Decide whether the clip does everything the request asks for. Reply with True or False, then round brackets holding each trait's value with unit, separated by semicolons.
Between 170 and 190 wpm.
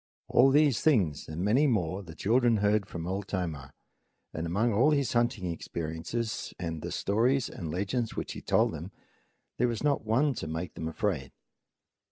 True (175 wpm)